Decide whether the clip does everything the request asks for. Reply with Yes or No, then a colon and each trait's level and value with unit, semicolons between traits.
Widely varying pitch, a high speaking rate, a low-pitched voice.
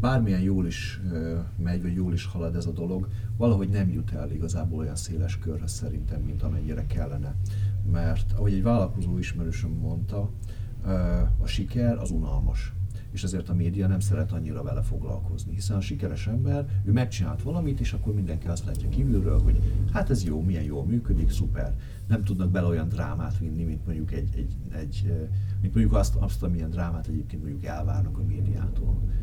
No: narrow, 2.5 semitones; fast, 175 wpm; very low, 95 Hz